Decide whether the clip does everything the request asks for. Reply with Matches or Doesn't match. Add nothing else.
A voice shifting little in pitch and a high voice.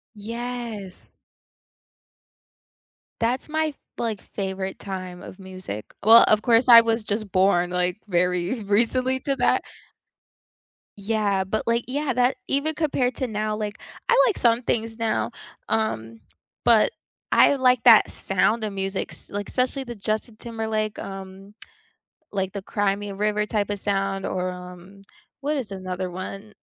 Doesn't match